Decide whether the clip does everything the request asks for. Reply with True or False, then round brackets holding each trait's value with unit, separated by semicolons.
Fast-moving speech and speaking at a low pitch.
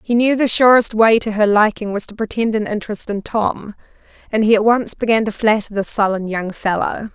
False (220 wpm; 215 Hz)